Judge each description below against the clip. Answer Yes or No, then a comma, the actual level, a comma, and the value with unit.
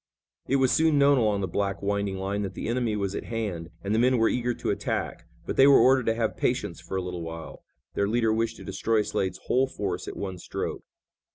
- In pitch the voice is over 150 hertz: No, low, 105 Hz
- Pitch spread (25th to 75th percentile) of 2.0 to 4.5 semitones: Yes, average, 4.0 semitones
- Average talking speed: No, fast, 235 wpm